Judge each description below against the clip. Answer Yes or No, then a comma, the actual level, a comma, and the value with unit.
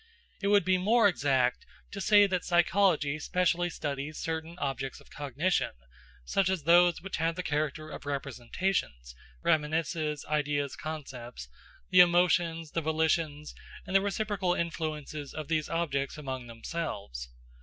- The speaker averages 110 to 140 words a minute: Yes, slow, 135 wpm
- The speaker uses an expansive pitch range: No, average, 3.7 semitones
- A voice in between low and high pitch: Yes, medium, 160 Hz